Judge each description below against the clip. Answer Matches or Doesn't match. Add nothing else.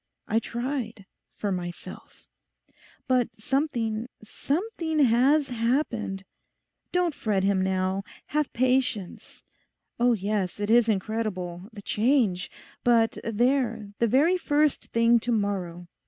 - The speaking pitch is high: Matches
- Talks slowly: Matches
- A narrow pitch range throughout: Doesn't match